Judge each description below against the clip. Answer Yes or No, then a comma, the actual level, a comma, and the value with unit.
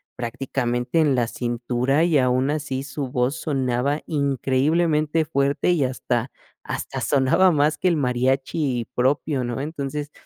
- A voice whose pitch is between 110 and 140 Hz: Yes, low, 135 Hz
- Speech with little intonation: No, average, 3.0 semitones